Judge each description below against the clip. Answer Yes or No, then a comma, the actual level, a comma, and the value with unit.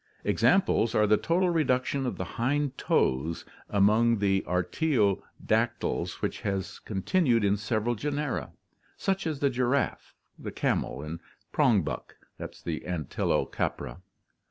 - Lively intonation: Yes, wide, 6.0 semitones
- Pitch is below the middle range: Yes, low, 115 Hz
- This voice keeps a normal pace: No, slow, 125 wpm